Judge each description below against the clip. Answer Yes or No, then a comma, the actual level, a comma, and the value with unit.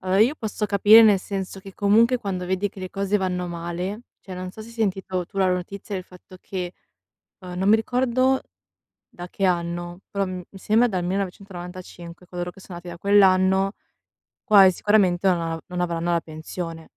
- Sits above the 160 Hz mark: Yes, medium, 185 Hz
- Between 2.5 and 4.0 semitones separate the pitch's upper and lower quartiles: No, narrow, 2.1 semitones